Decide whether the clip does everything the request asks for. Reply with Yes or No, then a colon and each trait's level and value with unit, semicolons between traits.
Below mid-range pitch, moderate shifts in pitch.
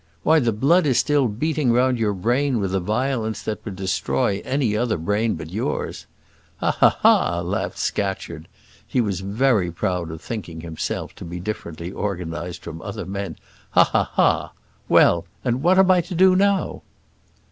No: low, 105 Hz; wide, 6.7 semitones